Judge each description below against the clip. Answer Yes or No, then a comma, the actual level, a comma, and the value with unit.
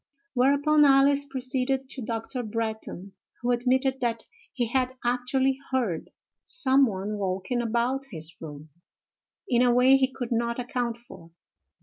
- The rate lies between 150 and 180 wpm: No, slow, 135 wpm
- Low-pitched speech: No, high, 245 Hz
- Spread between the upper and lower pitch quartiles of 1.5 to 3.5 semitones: Yes, average, 2.8 semitones